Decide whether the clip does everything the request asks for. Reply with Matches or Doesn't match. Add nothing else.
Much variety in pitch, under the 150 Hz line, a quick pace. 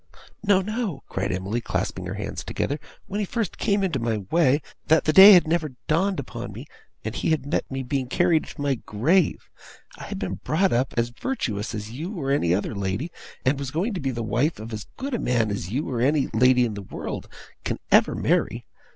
Matches